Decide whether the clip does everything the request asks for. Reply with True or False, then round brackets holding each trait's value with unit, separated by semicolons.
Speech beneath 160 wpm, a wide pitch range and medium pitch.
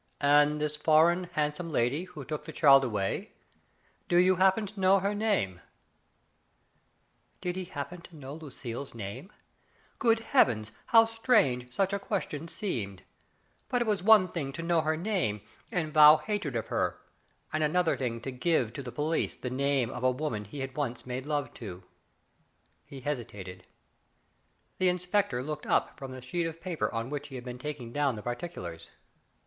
False (175 wpm; 6.2 semitones; 150 Hz)